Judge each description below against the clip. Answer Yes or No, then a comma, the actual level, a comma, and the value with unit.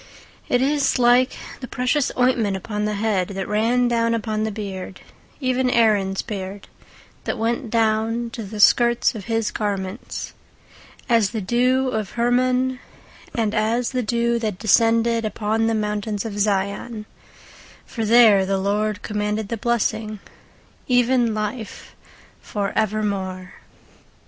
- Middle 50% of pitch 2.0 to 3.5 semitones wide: Yes, narrow, 2.4 semitones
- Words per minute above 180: No, average, 140 wpm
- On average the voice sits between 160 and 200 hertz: No, high, 220 Hz